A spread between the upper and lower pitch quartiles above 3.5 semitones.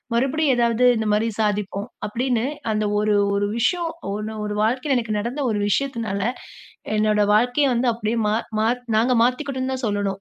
No: average, 3.2 semitones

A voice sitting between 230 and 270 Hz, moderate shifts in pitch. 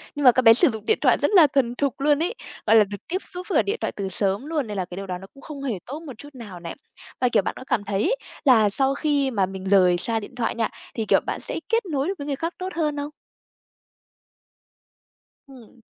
No: very high, 255 Hz; wide, 6.1 semitones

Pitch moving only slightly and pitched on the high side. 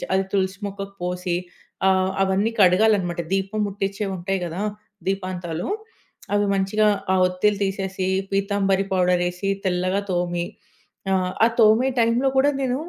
Yes: narrow, 1.8 semitones; high, 195 Hz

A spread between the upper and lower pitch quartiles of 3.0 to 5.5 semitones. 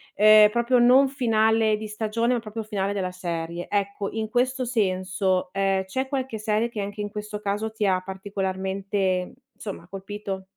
No: narrow, 2.6 semitones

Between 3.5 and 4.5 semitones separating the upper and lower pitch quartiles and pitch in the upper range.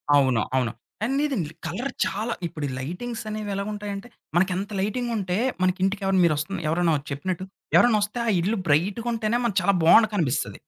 Yes: average, 4.2 semitones; high, 195 Hz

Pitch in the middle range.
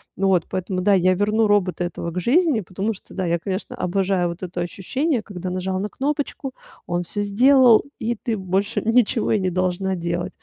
No: high, 195 Hz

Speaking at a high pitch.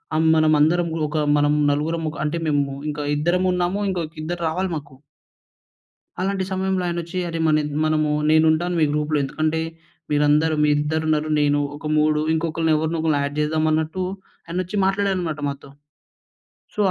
No: medium, 155 Hz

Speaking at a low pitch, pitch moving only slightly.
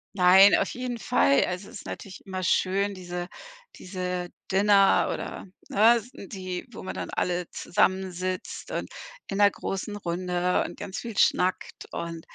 No: medium, 185 Hz; narrow, 2.0 semitones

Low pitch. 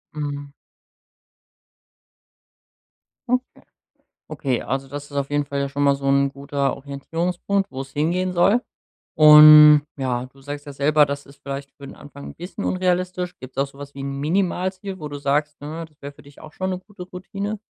No: medium, 145 Hz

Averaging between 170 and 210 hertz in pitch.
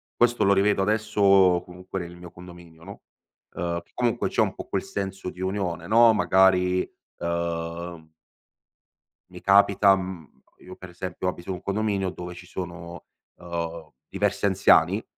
No: very low, 90 Hz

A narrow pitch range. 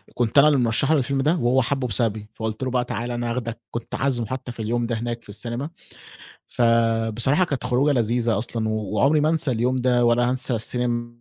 Yes: narrow, 2.1 semitones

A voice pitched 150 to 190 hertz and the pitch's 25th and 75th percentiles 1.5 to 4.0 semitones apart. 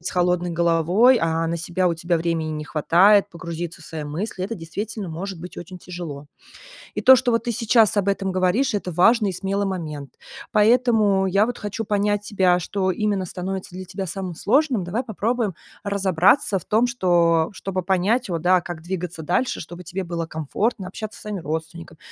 Yes: medium, 185 Hz; average, 3.5 semitones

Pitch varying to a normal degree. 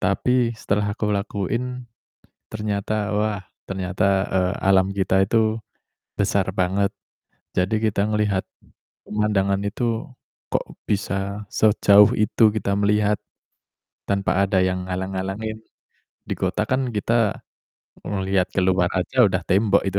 No: narrow, 2.0 semitones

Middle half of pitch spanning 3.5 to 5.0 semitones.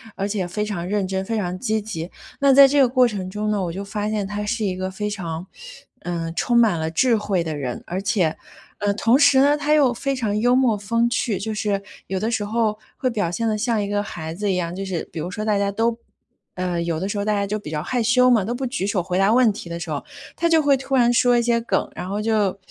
Yes: average, 4.0 semitones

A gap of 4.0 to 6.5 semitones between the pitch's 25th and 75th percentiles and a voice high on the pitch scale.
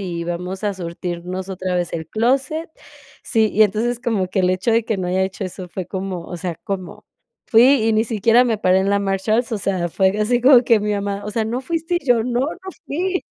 Yes: average, 4.3 semitones; high, 205 Hz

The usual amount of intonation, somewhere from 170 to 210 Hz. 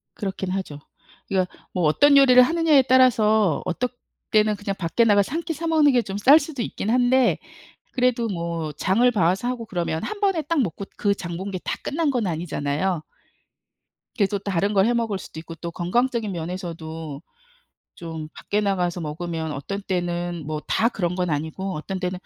No: wide, 6.1 semitones; high, 195 Hz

